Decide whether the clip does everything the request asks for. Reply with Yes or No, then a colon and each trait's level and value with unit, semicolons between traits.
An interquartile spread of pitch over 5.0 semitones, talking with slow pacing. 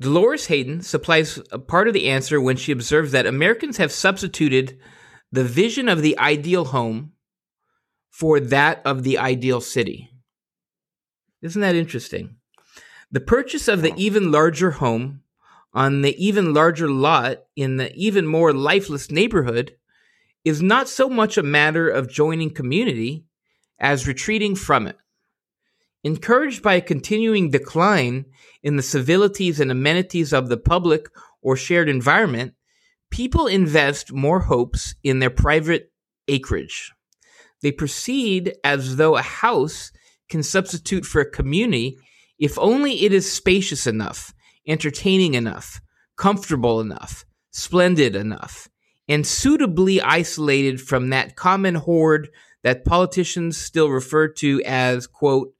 Yes: wide, 5.5 semitones; slow, 130 wpm